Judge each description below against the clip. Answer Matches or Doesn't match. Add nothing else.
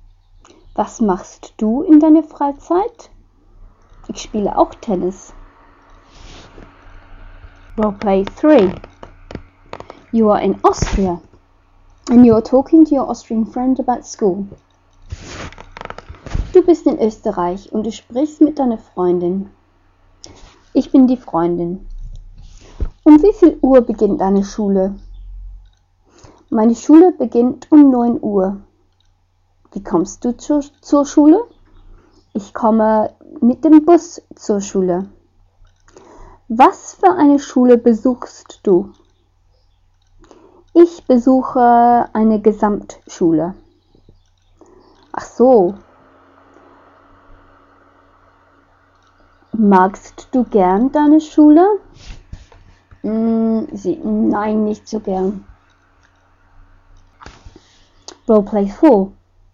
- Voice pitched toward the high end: Matches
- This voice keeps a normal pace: Doesn't match